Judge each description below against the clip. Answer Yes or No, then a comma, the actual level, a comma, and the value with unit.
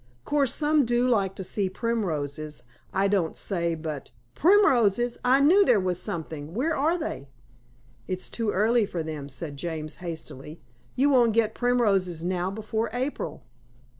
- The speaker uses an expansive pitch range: Yes, wide, 6.8 semitones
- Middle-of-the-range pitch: No, high, 200 Hz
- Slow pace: No, average, 155 wpm